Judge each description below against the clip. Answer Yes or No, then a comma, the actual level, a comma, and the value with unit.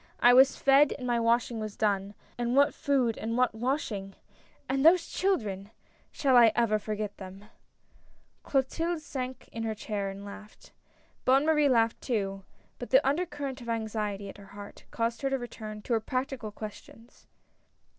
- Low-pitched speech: No, high, 235 Hz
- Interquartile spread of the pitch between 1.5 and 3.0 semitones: No, average, 4.2 semitones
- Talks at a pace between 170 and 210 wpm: Yes, average, 185 wpm